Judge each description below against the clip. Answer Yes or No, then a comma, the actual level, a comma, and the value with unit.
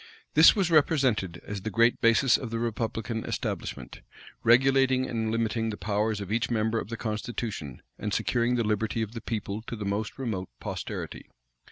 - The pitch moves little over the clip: Yes, narrow, 2.1 semitones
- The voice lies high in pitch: No, low, 115 Hz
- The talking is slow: No, average, 175 wpm